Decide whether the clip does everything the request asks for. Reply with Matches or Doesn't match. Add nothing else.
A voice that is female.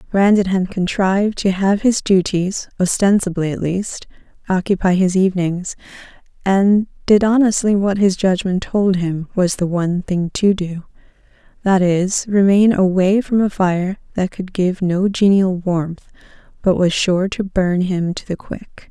Matches